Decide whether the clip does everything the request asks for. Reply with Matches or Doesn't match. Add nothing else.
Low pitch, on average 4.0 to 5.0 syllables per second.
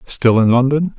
Matches